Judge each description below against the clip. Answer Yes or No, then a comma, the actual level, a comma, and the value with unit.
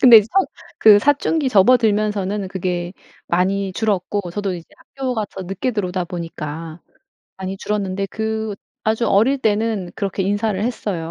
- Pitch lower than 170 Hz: No, high, 205 Hz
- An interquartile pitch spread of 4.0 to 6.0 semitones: No, average, 3.0 semitones